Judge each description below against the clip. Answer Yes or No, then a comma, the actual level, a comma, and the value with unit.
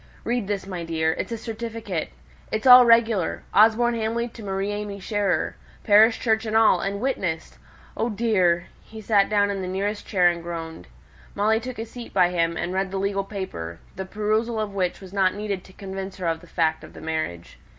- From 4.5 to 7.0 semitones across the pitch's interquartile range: No, average, 3.5 semitones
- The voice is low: No, high, 200 Hz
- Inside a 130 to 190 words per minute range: No, average, 200 wpm